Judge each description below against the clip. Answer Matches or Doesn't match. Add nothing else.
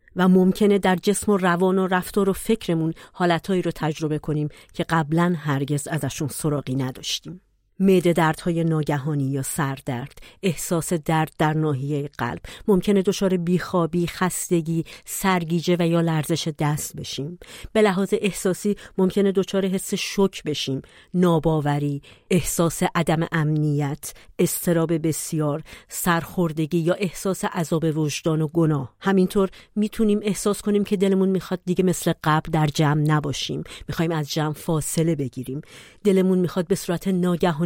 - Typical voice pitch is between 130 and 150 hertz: Doesn't match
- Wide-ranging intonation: Doesn't match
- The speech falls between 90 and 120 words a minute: Doesn't match